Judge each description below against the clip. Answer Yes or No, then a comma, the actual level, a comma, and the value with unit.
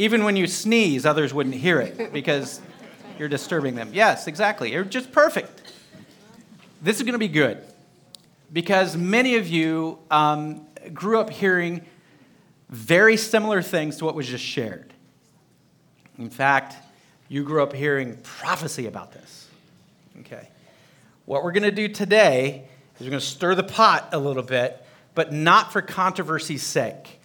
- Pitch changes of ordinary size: No, wide, 6.2 semitones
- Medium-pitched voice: Yes, medium, 165 Hz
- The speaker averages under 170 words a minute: Yes, average, 150 wpm